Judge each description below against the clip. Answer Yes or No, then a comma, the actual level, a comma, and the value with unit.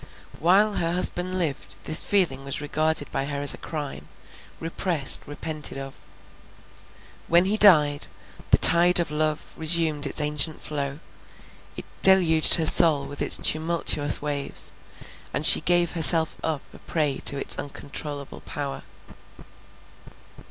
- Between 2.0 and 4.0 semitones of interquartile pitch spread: Yes, average, 2.9 semitones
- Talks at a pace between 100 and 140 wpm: Yes, slow, 135 wpm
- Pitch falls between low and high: Yes, medium, 155 Hz